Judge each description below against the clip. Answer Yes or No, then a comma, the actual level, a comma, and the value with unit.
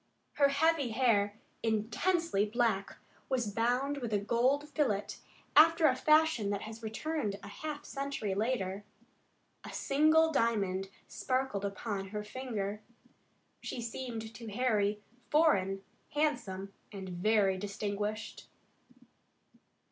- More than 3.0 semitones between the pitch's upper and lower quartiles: Yes, wide, 5.4 semitones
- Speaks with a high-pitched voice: Yes, high, 225 Hz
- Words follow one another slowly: Yes, slow, 110 wpm